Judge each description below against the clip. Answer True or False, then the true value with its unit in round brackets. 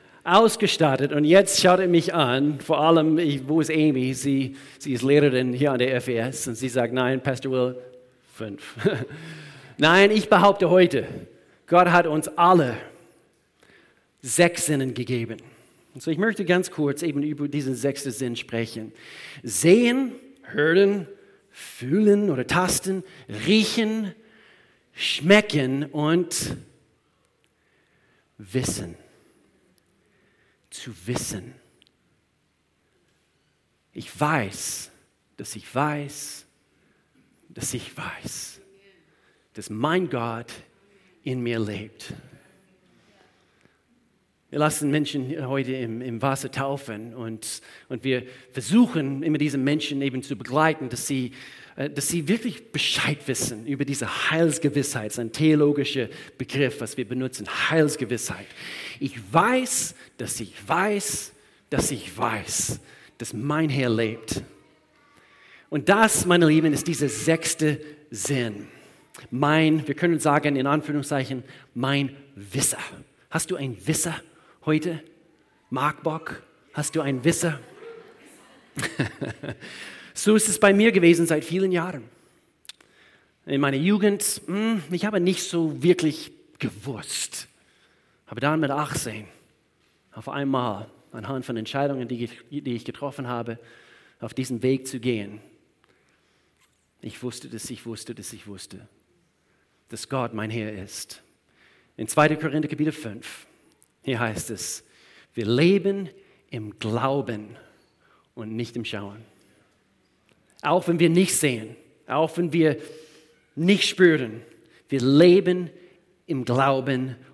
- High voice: False (140 Hz)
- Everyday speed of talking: False (120 wpm)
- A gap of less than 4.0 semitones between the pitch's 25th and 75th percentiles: False (5.0 semitones)